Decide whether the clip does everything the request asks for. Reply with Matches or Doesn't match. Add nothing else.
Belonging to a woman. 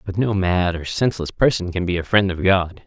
Doesn't match